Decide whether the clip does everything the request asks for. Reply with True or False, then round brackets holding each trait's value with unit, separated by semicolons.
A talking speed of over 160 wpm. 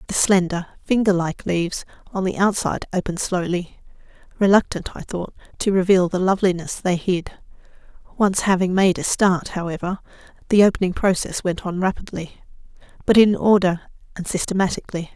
False (140 wpm)